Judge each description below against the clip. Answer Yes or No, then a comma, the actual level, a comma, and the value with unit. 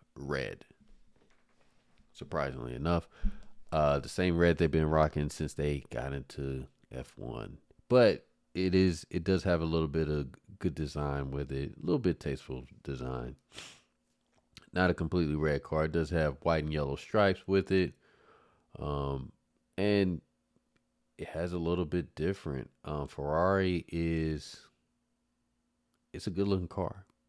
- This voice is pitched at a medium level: No, very low, 75 Hz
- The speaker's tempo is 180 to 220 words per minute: No, average, 140 wpm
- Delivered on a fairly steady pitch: No, average, 4.3 semitones